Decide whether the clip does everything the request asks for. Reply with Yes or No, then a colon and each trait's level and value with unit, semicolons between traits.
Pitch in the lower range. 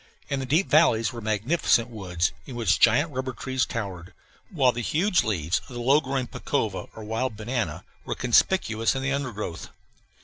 Yes: low, 120 Hz